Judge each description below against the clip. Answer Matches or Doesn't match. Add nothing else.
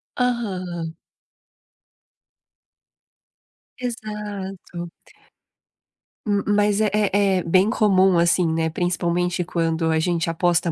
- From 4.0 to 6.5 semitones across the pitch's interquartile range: Doesn't match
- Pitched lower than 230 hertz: Matches